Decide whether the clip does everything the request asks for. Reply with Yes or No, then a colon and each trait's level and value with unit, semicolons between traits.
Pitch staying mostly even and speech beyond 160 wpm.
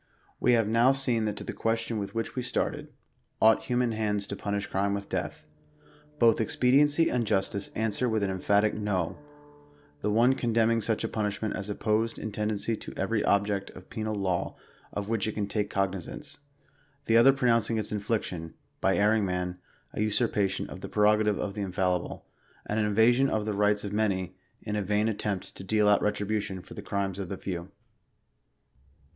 Yes: narrow, 2.2 semitones; average, 195 wpm